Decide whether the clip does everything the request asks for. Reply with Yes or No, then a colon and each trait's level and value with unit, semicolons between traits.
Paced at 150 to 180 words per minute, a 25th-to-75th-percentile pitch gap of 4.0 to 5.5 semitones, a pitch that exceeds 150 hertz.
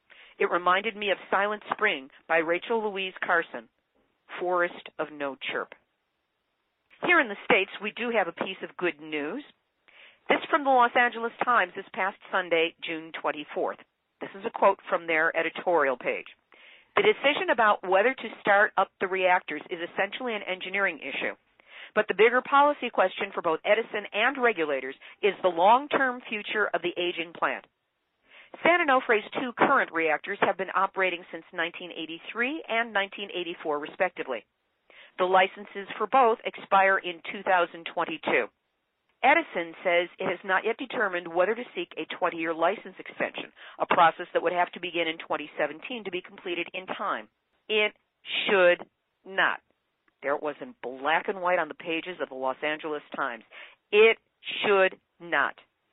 Yes: average, 155 wpm; average, 4.3 semitones; high, 190 Hz